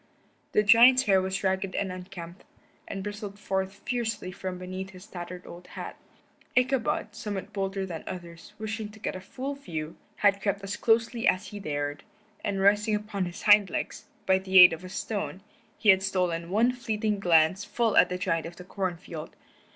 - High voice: Yes, high, 195 Hz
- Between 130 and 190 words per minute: Yes, average, 185 wpm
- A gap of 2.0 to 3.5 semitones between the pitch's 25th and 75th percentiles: Yes, narrow, 2.5 semitones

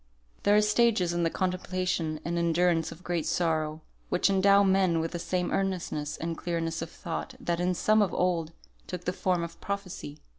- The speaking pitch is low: No, medium, 175 Hz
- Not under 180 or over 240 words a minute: Yes, average, 185 wpm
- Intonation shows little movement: Yes, narrow, 2.3 semitones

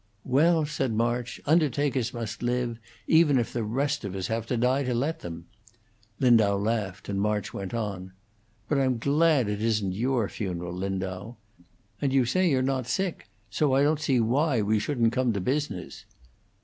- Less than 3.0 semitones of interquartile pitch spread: No, average, 4.9 semitones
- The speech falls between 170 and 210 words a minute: Yes, average, 175 wpm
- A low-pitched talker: Yes, low, 120 Hz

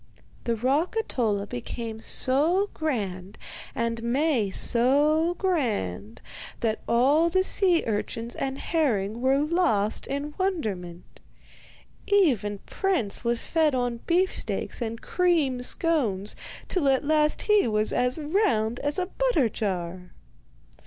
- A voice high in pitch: Yes, very high, 255 Hz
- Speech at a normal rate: No, slow, 120 wpm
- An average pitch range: No, wide, 6.9 semitones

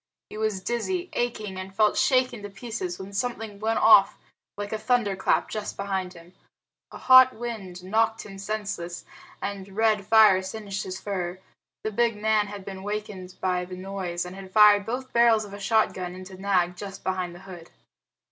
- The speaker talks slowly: No, average, 175 wpm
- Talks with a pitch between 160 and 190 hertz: No, high, 200 Hz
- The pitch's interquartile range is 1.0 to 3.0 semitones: Yes, average, 2.7 semitones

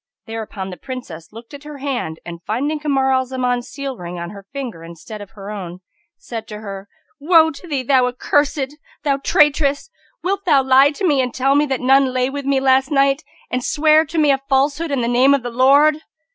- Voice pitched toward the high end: Yes, very high, 265 Hz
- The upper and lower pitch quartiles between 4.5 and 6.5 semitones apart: No, average, 3.6 semitones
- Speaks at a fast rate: Yes, fast, 215 wpm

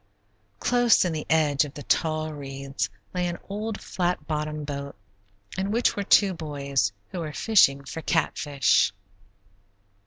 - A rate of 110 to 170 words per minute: Yes, average, 145 wpm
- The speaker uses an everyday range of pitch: Yes, average, 4.2 semitones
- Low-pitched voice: No, medium, 155 Hz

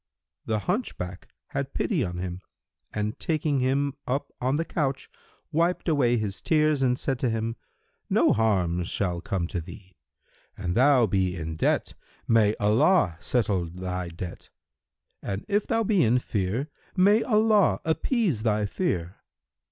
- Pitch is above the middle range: No, low, 115 Hz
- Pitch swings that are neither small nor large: No, wide, 8.5 semitones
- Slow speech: No, average, 145 wpm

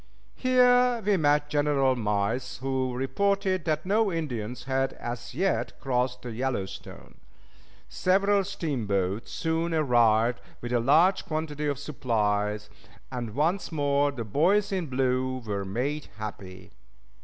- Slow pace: Yes, slow, 125 wpm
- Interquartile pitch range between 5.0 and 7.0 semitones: Yes, wide, 5.5 semitones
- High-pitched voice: No, low, 135 Hz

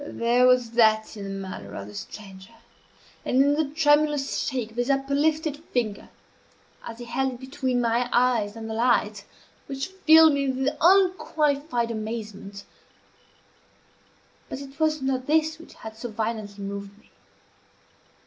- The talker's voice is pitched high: Yes, very high, 250 Hz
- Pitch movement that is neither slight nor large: Yes, average, 4.8 semitones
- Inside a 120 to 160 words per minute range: Yes, average, 150 wpm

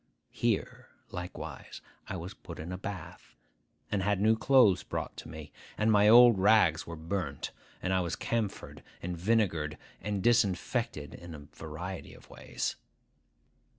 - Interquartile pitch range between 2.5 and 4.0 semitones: No, average, 4.4 semitones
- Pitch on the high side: No, very low, 95 Hz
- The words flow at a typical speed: Yes, average, 150 wpm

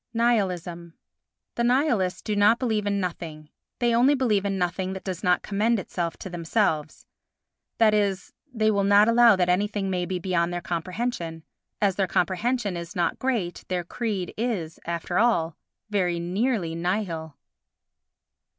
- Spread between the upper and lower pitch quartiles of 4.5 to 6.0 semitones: No, average, 4.0 semitones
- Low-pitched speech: No, high, 190 Hz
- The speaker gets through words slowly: No, average, 150 wpm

